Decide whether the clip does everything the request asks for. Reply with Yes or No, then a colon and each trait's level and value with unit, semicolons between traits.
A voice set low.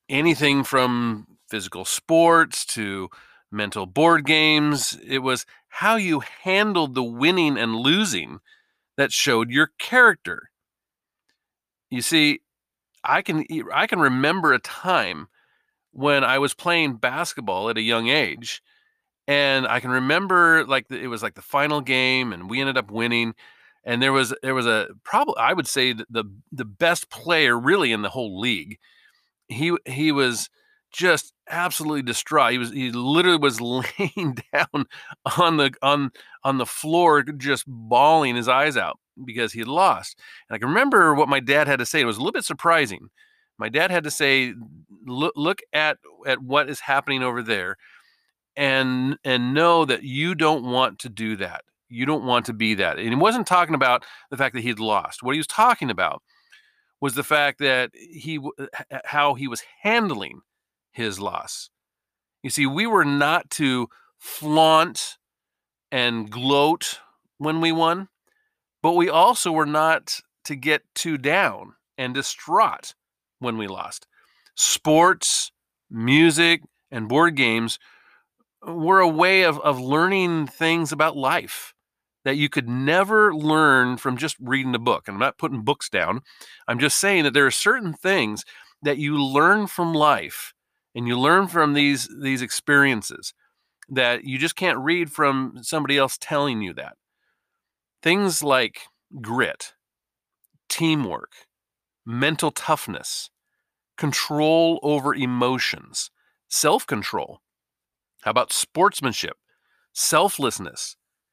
No: medium, 145 Hz